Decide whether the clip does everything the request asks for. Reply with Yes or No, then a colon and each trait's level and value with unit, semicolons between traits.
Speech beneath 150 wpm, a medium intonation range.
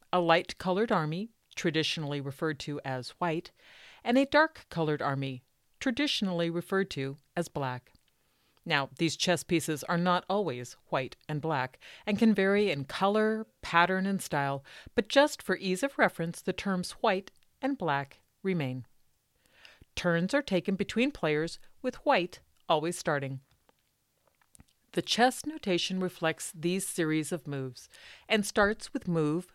Yes: average, 140 wpm; average, 5.0 semitones